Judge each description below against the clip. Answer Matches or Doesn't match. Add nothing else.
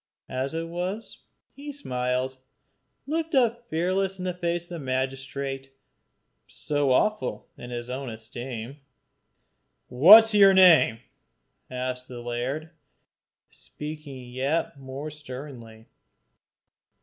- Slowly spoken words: Matches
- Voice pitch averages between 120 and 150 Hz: Matches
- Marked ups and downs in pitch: Matches